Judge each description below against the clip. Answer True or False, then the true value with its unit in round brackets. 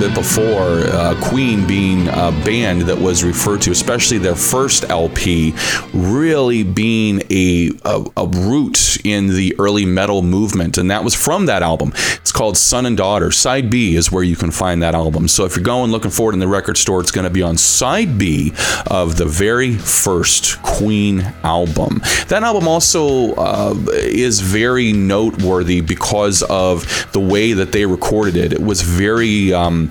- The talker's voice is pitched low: True (95 Hz)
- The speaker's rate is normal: True (175 wpm)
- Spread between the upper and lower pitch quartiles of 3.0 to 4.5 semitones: True (3.3 semitones)